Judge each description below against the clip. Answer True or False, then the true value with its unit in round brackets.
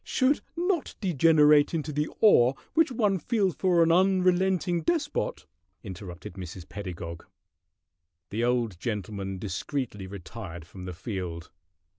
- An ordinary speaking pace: False (120 wpm)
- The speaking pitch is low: True (130 Hz)